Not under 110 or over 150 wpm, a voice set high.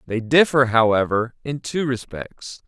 No: slow, 135 wpm; low, 125 Hz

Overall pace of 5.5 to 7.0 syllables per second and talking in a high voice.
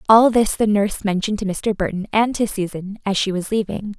Yes: 5.7 syllables/s; high, 205 Hz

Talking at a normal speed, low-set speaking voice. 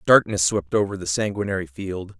Yes: average, 165 wpm; very low, 95 Hz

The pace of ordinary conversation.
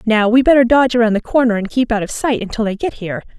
No: fast, 285 wpm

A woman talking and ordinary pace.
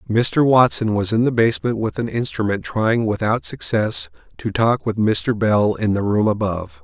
No: male; average, 185 wpm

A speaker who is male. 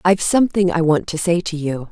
No: female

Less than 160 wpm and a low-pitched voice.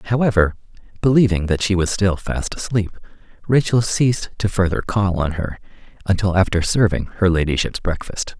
Yes: average, 150 wpm; very low, 95 Hz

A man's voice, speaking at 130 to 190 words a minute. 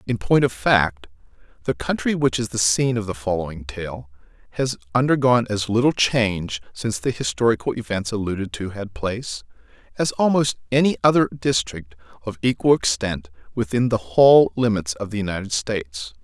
Yes: male; average, 160 wpm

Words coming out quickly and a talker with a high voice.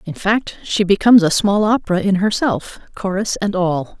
No: average, 180 wpm; high, 195 Hz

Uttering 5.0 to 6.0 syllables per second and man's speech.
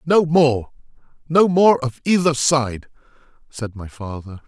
No: 3.9 syllables/s; male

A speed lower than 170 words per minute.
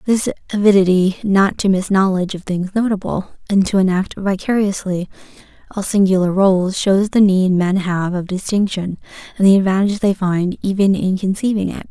Yes: average, 160 wpm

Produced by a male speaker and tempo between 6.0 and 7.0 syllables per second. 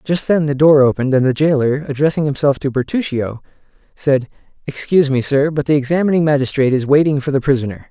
Yes: male; 6.4 syllables/s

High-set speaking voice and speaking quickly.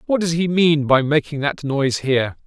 No: medium, 150 Hz; fast, 220 wpm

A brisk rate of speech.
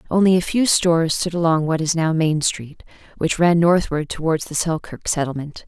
No: average, 190 wpm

